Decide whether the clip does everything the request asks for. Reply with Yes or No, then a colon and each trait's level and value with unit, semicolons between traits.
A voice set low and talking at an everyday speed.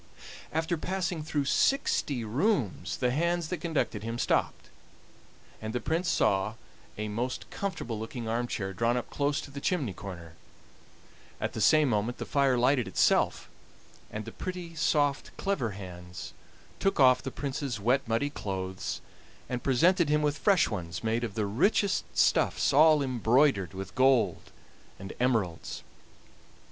Yes: low, 125 Hz; average, 150 wpm